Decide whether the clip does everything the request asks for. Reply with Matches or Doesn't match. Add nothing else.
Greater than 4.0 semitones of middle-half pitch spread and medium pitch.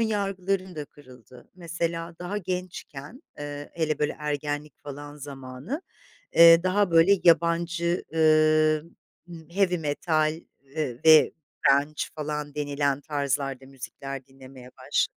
Doesn't match